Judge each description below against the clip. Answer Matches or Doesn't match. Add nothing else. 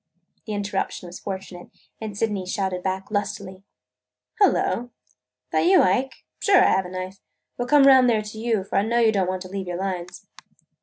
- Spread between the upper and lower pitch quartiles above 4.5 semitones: Doesn't match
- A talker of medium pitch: Doesn't match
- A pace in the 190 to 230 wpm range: Matches